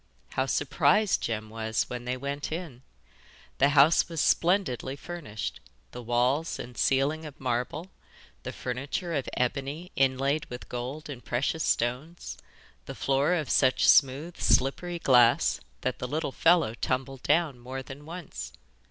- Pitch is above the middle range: No, low, 135 Hz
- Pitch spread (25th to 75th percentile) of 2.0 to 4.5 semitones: Yes, average, 4.1 semitones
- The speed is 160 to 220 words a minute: No, average, 145 wpm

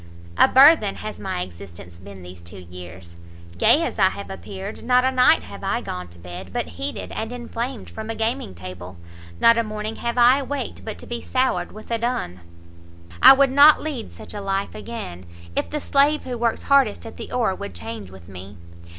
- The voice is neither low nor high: No, high, 210 Hz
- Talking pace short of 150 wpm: No, average, 200 wpm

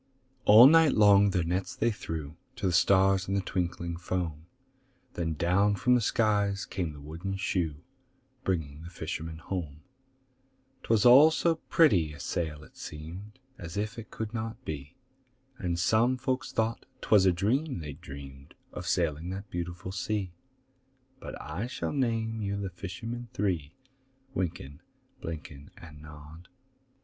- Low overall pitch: Yes, very low, 90 Hz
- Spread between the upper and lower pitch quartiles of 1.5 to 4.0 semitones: No, average, 4.8 semitones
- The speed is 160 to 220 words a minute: No, average, 150 wpm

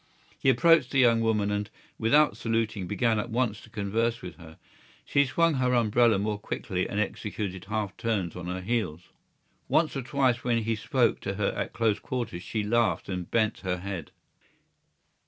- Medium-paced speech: Yes, average, 175 wpm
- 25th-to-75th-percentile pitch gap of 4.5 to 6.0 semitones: No, average, 3.2 semitones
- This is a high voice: No, low, 110 Hz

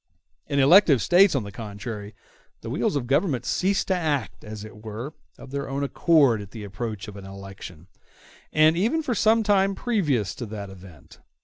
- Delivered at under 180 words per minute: No, average, 185 wpm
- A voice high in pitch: No, low, 130 Hz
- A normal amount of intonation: No, wide, 8.7 semitones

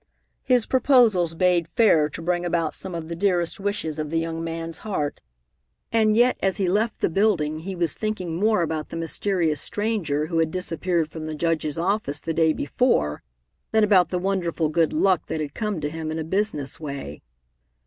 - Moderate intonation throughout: Yes, average, 4.0 semitones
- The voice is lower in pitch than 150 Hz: No, medium, 170 Hz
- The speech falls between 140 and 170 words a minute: No, average, 190 wpm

